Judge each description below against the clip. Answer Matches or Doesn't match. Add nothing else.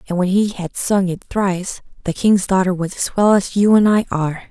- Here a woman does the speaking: Matches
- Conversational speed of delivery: Doesn't match